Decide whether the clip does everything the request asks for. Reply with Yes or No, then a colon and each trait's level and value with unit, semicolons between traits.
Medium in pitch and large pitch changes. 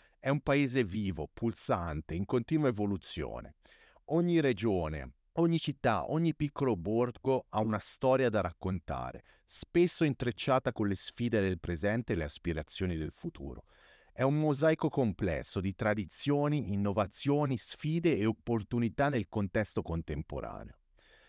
No: low, 115 Hz; wide, 6.4 semitones